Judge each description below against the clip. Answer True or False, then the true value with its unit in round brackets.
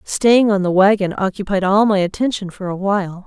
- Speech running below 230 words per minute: True (200 wpm)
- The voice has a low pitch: False (195 Hz)